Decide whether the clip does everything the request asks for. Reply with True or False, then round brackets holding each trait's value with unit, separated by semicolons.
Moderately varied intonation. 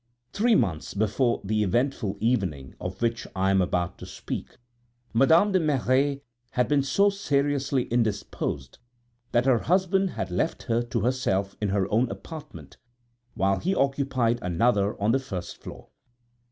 False (6.0 semitones)